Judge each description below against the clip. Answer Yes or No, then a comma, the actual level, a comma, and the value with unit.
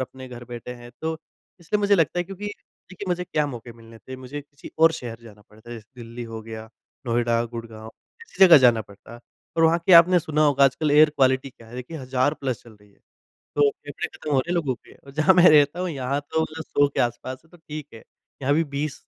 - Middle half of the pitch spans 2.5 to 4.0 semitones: No, average, 5.1 semitones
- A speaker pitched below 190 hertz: Yes, medium, 140 Hz